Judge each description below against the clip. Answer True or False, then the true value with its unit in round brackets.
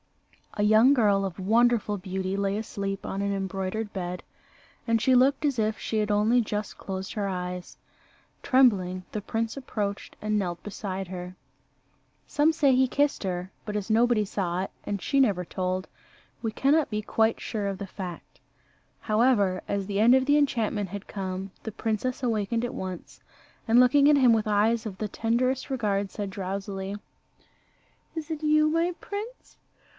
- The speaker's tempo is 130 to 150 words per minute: False (170 wpm)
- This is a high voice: True (210 Hz)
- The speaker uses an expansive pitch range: False (4.0 semitones)